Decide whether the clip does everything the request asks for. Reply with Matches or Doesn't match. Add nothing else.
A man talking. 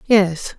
Doesn't match